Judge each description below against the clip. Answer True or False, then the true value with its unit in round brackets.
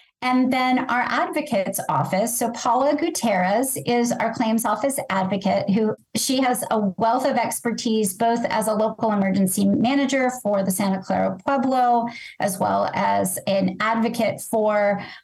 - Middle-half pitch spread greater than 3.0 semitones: True (3.7 semitones)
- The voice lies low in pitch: False (225 Hz)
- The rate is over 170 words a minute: False (145 wpm)